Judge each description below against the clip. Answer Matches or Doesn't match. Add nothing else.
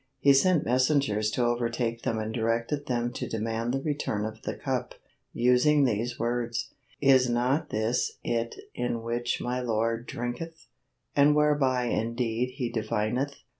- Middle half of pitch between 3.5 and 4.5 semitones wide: Doesn't match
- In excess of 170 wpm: Doesn't match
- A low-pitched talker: Matches